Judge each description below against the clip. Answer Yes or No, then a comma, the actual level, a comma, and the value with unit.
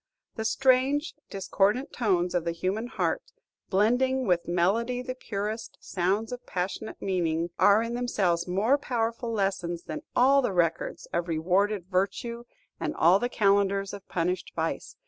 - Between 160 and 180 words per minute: No, average, 145 wpm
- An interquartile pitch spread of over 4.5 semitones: Yes, average, 5.0 semitones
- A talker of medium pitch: No, high, 200 Hz